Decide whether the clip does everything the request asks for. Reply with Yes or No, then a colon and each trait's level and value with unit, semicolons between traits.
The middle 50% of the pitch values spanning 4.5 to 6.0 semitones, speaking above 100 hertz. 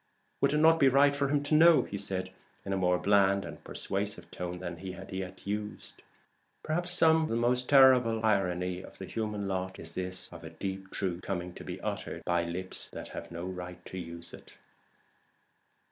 No: wide, 5.6 semitones; very low, 95 Hz